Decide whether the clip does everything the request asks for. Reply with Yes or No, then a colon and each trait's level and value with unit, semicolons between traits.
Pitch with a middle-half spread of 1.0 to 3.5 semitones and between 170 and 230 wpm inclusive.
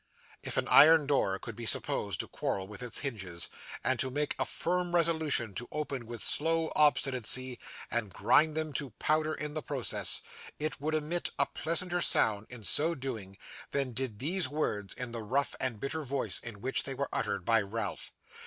No: average, 5.3 semitones; average, 185 wpm